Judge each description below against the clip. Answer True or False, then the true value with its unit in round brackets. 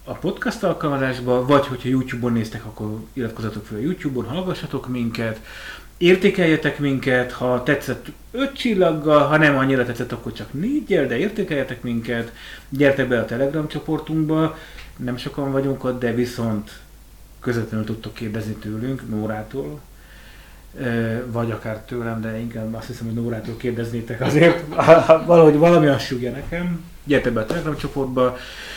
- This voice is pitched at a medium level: False (125 Hz)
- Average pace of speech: True (140 wpm)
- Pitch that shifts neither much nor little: True (4.8 semitones)